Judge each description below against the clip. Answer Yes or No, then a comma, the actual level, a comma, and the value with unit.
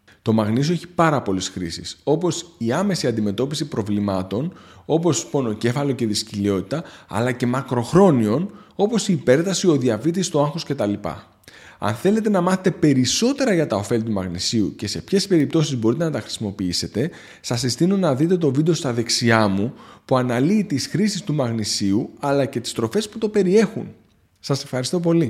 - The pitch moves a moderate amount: No, wide, 7.5 semitones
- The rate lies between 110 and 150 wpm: No, average, 165 wpm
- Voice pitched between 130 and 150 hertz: Yes, medium, 140 Hz